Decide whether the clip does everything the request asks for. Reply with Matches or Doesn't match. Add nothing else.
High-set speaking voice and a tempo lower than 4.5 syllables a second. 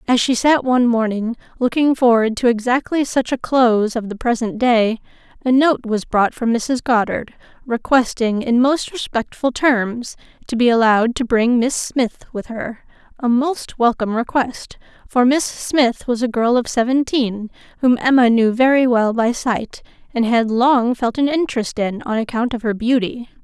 Doesn't match